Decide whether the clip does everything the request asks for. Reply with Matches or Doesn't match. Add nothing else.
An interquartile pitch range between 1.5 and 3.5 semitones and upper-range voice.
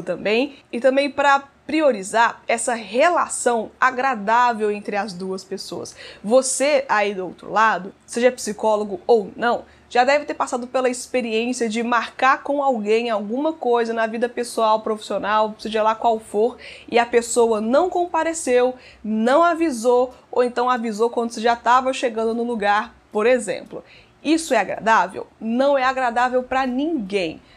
Matches